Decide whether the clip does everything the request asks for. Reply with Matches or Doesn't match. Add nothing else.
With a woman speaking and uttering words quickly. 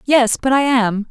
Matches